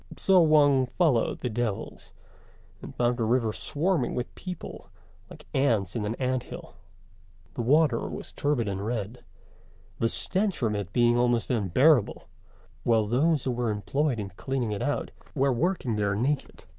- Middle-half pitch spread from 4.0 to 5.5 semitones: Yes, average, 4.4 semitones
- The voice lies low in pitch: Yes, low, 120 Hz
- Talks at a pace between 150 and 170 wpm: Yes, average, 155 wpm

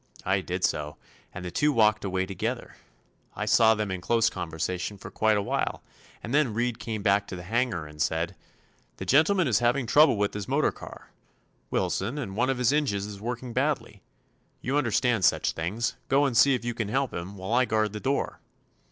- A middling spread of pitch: Yes, average, 4.5 semitones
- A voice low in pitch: Yes, low, 110 Hz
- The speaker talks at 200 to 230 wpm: Yes, fast, 205 wpm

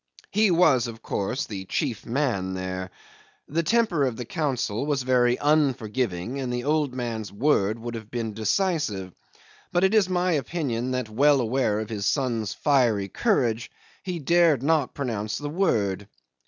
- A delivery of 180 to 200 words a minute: No, average, 160 wpm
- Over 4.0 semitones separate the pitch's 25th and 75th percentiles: Yes, wide, 5.5 semitones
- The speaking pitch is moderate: No, low, 125 Hz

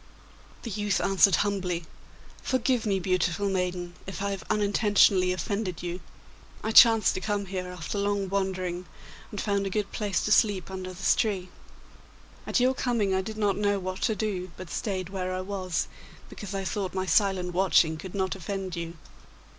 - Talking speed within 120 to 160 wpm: No, average, 175 wpm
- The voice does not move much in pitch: Yes, narrow, 1.9 semitones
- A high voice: Yes, high, 195 Hz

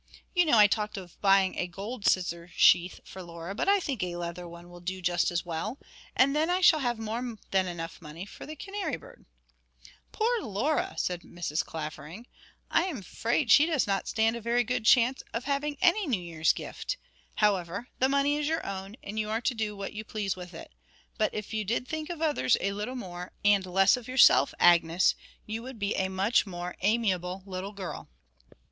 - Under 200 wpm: No, fast, 205 wpm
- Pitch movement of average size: No, wide, 6.0 semitones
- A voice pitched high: Yes, high, 210 Hz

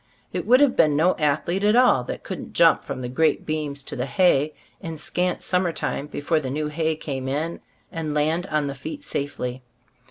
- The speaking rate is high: Yes, fast, 210 wpm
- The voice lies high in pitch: No, medium, 155 Hz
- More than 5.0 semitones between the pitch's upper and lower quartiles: No, average, 3.6 semitones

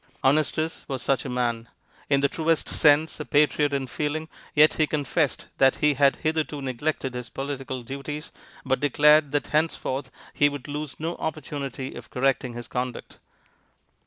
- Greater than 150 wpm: Yes, average, 160 wpm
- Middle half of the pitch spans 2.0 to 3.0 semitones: Yes, narrow, 2.4 semitones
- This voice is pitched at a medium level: Yes, medium, 145 Hz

